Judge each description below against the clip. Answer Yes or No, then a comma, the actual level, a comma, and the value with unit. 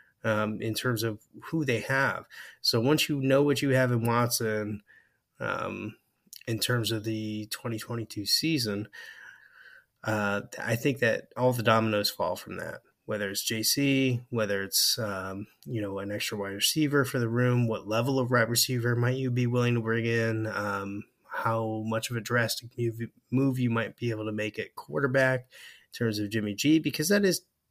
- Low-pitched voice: Yes, low, 115 Hz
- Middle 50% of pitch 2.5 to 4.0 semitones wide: Yes, average, 2.8 semitones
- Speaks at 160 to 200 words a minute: Yes, average, 180 wpm